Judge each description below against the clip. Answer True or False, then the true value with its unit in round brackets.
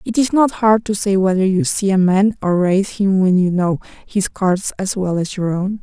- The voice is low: False (195 Hz)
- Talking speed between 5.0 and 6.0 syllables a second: False (4.8 syllables/s)